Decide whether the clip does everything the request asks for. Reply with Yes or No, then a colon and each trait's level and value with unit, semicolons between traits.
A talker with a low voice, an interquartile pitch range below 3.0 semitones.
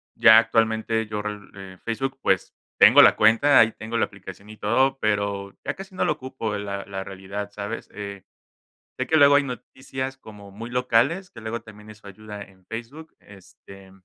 No: low, 110 Hz; average, 3.8 semitones